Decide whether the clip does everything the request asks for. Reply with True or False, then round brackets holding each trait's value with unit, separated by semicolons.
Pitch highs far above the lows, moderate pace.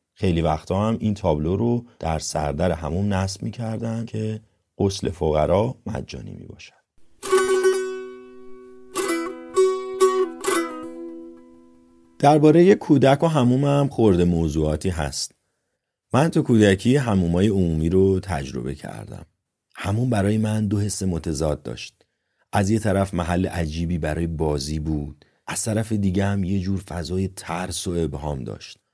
True (6.2 semitones; 125 wpm)